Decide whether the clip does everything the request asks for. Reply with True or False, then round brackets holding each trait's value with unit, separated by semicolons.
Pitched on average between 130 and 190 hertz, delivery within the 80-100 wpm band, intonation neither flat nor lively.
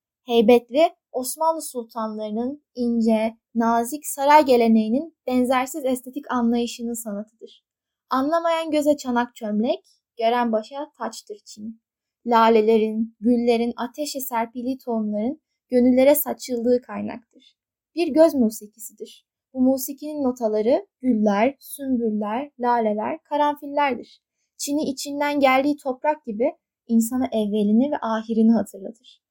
False (245 Hz; 95 wpm; 4.1 semitones)